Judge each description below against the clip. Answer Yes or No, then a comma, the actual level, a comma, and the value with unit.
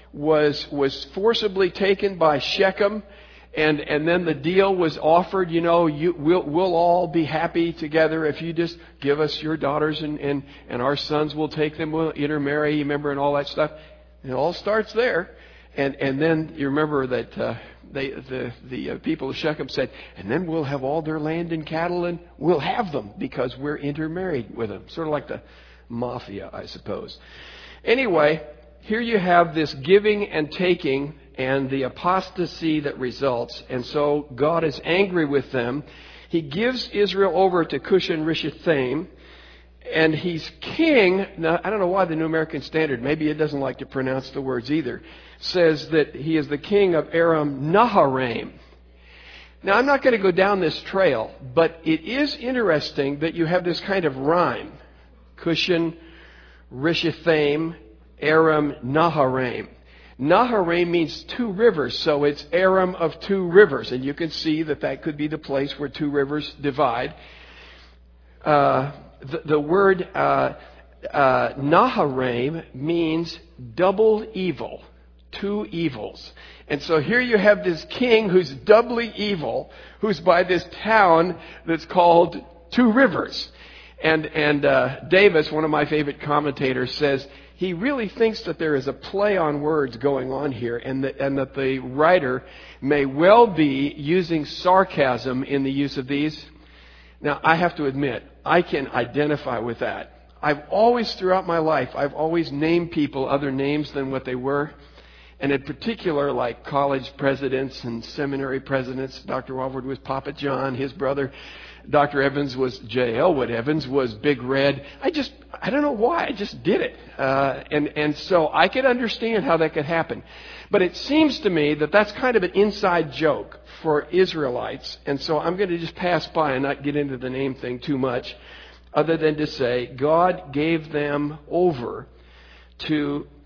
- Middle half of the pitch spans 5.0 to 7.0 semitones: No, average, 4.1 semitones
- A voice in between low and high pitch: Yes, medium, 155 Hz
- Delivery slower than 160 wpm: No, average, 170 wpm